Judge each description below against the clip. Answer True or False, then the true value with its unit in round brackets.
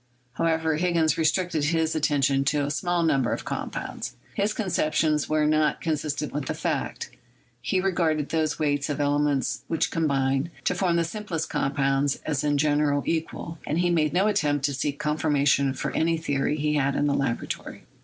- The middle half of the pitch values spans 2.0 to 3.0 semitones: True (2.4 semitones)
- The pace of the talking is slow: False (175 wpm)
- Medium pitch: True (150 Hz)